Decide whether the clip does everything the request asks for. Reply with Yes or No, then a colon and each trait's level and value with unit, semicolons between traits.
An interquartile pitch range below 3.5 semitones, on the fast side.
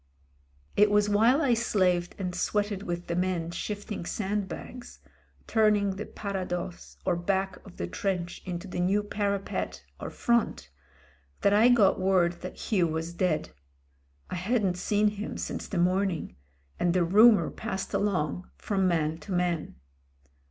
No: average, 2.9 semitones; average, 150 wpm